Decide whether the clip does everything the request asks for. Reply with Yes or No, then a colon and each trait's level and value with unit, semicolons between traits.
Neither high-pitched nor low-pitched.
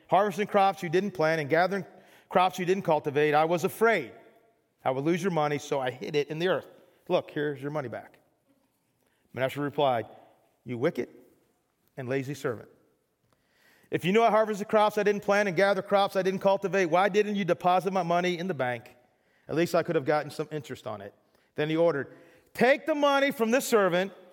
Yes: medium, 180 Hz